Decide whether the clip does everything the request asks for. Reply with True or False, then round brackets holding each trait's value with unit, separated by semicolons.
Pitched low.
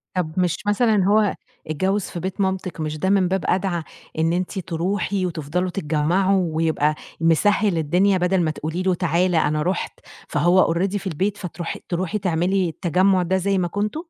False (180 Hz)